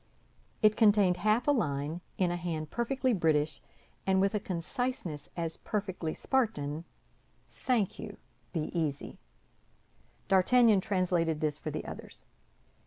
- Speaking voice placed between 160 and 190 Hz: Yes, medium, 185 Hz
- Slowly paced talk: Yes, slow, 125 wpm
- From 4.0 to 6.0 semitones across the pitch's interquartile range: Yes, average, 5.1 semitones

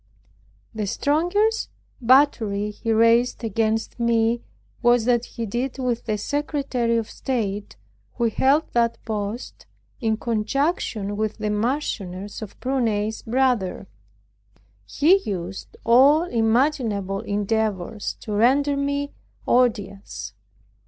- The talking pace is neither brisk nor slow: No, slow, 105 wpm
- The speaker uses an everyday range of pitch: Yes, average, 3.8 semitones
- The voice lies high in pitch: Yes, high, 230 Hz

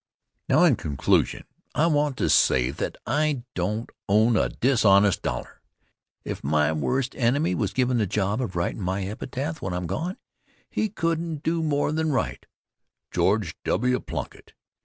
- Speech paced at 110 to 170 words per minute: Yes, average, 155 wpm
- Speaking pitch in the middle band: No, low, 120 Hz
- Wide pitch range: Yes, wide, 7.7 semitones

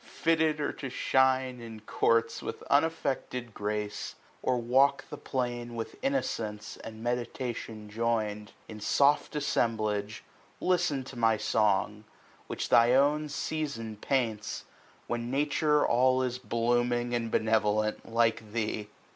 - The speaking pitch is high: No, low, 120 Hz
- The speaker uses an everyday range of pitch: Yes, average, 3.2 semitones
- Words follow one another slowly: Yes, slow, 125 wpm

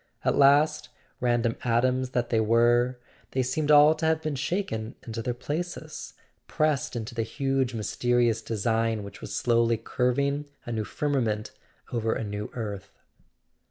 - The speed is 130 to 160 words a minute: Yes, average, 150 wpm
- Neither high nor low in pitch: No, low, 120 Hz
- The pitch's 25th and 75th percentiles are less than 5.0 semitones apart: Yes, average, 3.6 semitones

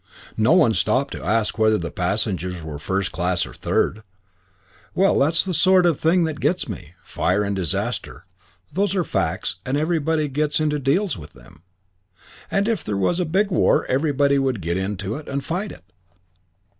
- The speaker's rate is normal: Yes, average, 180 wpm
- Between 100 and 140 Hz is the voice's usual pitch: Yes, low, 135 Hz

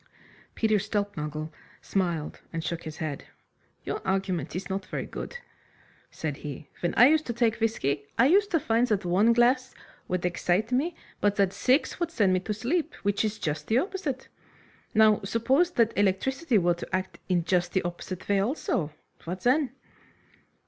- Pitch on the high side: Yes, high, 205 Hz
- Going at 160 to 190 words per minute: Yes, average, 170 wpm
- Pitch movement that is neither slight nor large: No, wide, 5.8 semitones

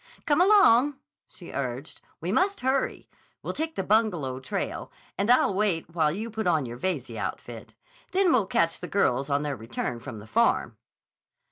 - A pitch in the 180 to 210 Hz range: Yes, medium, 185 Hz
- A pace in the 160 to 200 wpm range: Yes, average, 170 wpm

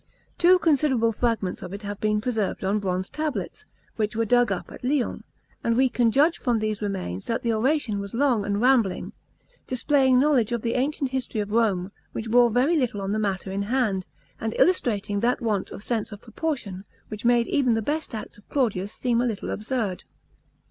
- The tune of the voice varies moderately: Yes, average, 3.8 semitones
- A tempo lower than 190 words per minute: No, average, 195 wpm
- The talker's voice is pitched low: No, high, 230 Hz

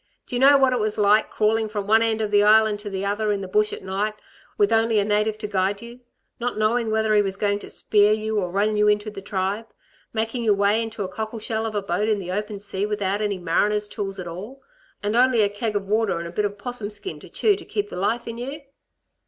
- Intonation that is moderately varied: No, narrow, 1.6 semitones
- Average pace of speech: No, fast, 260 wpm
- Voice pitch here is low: No, high, 210 Hz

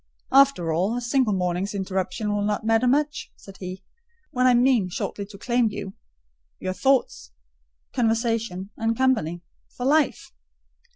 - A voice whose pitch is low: No, high, 215 Hz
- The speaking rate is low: Yes, slow, 130 wpm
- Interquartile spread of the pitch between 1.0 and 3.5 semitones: No, average, 4.9 semitones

